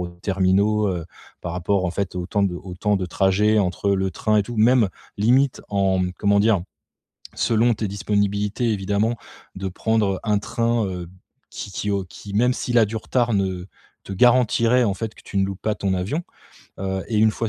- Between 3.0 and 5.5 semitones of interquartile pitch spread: No, narrow, 2.6 semitones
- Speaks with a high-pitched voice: No, low, 100 Hz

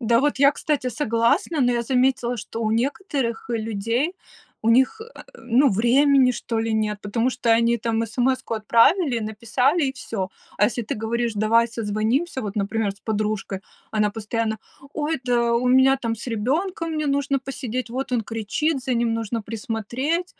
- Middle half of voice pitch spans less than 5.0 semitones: Yes, average, 3.2 semitones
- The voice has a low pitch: No, high, 235 Hz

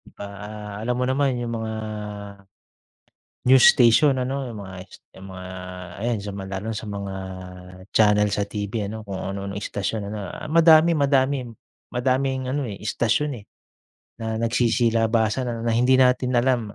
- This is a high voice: No, low, 115 Hz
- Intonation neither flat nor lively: Yes, average, 3.9 semitones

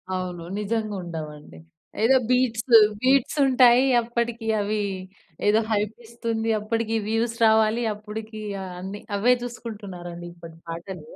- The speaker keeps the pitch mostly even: No, average, 3.6 semitones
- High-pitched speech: Yes, high, 220 Hz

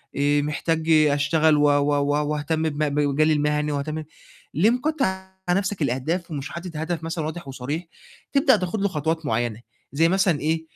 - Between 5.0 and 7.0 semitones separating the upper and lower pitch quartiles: No, average, 3.0 semitones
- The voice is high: No, medium, 155 Hz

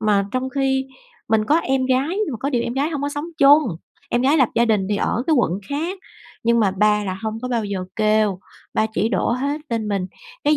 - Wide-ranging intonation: No, average, 4.8 semitones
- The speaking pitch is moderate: No, high, 240 Hz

